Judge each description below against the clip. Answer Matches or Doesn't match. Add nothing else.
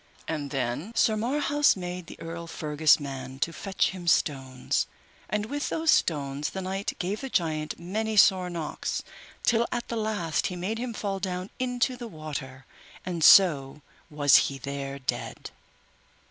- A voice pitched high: Doesn't match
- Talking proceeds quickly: Doesn't match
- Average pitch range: Doesn't match